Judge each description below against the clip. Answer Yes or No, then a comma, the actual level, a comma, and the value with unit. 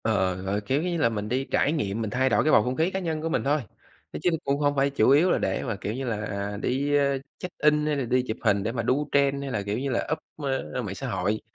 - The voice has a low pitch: Yes, low, 130 Hz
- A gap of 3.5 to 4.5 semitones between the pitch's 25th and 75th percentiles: No, average, 5.2 semitones